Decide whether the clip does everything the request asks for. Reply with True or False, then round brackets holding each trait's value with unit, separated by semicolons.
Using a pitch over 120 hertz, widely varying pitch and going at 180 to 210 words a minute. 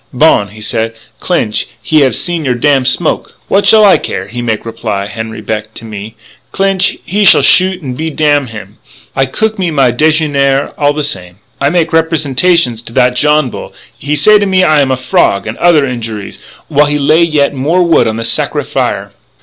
True (140 Hz; 6.2 semitones; 205 wpm)